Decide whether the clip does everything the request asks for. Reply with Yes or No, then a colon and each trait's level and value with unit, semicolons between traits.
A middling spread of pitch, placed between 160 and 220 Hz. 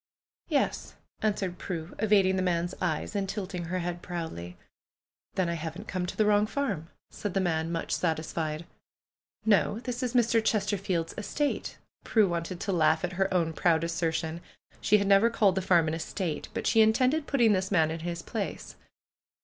Yes: average, 3.8 semitones; medium, 185 Hz